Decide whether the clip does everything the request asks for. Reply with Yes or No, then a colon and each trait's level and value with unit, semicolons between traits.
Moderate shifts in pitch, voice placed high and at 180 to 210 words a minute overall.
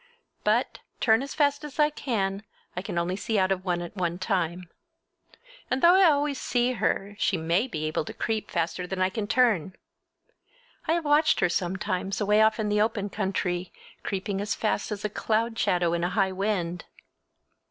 Yes: average, 4.0 semitones; high, 200 Hz; average, 190 wpm